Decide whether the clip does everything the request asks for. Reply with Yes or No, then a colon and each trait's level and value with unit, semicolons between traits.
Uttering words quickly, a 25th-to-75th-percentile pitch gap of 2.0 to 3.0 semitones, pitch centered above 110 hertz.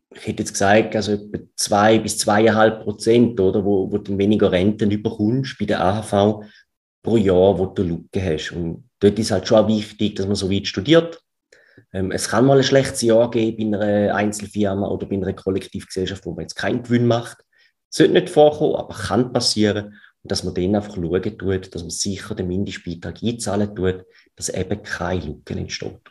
No: fast, 200 wpm; narrow, 2.6 semitones; low, 105 Hz